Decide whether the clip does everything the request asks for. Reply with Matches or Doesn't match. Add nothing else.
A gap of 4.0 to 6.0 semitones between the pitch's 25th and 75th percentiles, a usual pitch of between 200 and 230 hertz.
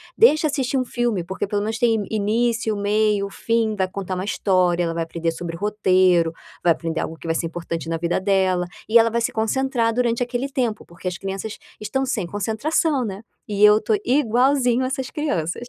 Matches